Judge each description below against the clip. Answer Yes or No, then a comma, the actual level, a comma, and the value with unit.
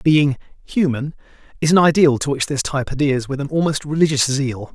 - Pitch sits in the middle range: Yes, medium, 145 Hz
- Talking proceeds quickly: No, average, 175 wpm